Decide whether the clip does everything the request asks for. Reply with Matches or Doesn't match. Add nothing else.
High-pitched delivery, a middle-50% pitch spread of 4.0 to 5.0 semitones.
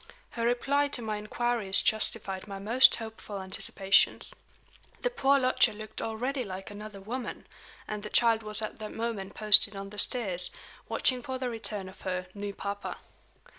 Doesn't match